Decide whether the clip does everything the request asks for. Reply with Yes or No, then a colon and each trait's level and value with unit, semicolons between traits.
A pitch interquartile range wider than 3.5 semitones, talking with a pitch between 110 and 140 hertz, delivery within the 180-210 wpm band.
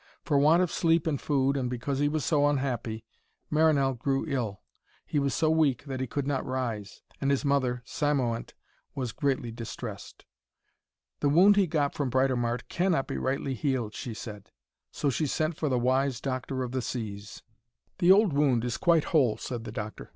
No: average, 3.2 semitones; low, 135 Hz; average, 185 wpm